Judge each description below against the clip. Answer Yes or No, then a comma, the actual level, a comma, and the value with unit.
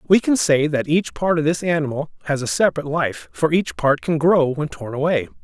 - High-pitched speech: No, medium, 155 Hz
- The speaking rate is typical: No, fast, 230 wpm